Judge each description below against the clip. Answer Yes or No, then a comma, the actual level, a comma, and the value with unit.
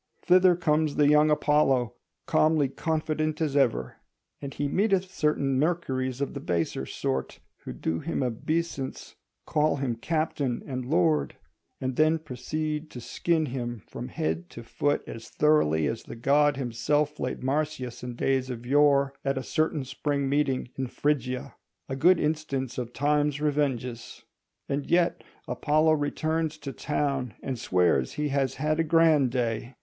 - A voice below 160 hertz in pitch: Yes, medium, 140 Hz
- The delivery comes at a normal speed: Yes, average, 155 wpm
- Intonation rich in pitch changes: No, average, 3.5 semitones